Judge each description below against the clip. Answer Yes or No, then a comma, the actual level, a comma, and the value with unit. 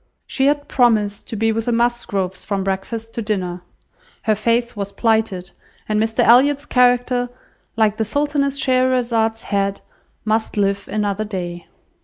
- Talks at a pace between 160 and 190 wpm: No, average, 145 wpm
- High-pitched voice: Yes, high, 220 Hz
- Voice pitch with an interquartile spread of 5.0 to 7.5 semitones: No, average, 3.4 semitones